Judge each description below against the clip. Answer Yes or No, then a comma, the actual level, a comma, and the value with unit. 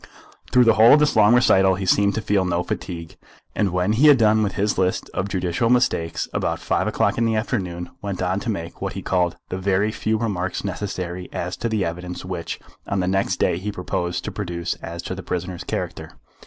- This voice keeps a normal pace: No, fast, 220 wpm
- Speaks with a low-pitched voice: Yes, very low, 95 Hz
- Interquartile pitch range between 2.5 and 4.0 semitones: Yes, average, 3.1 semitones